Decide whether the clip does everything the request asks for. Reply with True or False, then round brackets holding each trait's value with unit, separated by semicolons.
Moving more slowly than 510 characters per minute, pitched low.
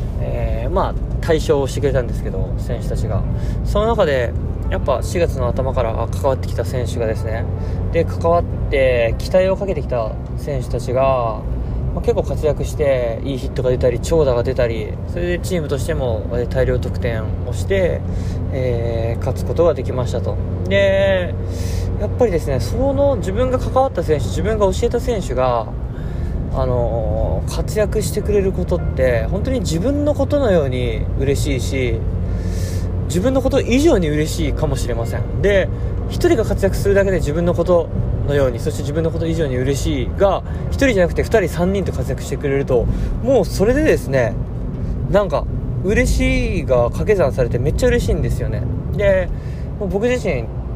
True (330 characters per minute; 100 Hz)